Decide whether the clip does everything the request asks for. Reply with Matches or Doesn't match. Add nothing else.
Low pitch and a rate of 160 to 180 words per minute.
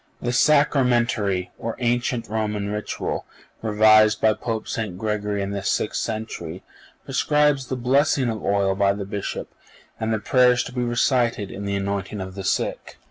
Matches